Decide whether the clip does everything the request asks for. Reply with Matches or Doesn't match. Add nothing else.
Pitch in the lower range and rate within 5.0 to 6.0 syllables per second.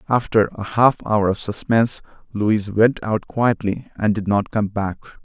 Doesn't match